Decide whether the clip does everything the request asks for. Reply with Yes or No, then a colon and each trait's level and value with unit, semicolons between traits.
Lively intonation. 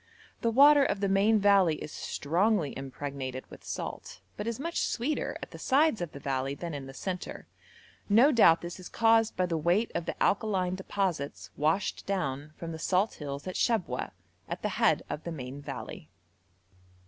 Yes: wide, 6.8 semitones